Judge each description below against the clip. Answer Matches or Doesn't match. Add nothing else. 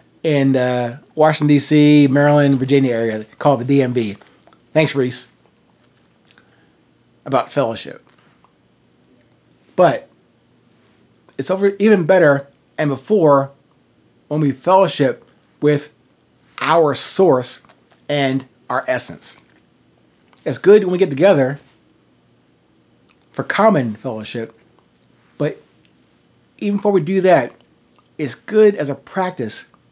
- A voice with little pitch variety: Doesn't match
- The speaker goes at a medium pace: Doesn't match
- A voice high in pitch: Doesn't match